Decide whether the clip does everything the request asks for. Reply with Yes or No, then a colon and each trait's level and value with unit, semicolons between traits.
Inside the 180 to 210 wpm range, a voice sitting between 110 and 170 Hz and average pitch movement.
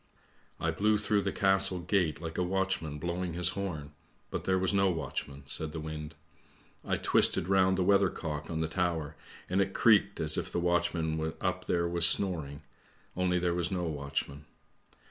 No: average, 190 wpm; very low, 85 Hz; average, 3.2 semitones